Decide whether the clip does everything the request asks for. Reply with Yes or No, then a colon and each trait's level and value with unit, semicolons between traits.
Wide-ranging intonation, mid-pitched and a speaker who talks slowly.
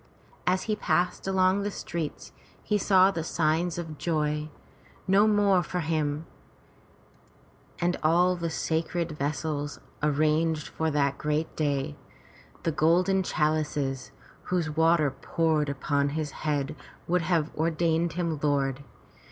No: average, 2.8 semitones; medium, 160 Hz; slow, 125 wpm